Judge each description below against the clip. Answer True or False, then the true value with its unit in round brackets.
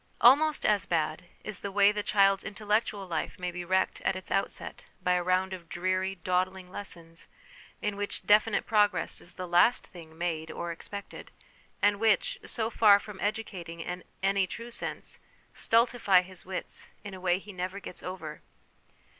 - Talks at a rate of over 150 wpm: True (170 wpm)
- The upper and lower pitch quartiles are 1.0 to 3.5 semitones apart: True (2.4 semitones)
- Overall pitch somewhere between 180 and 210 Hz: True (190 Hz)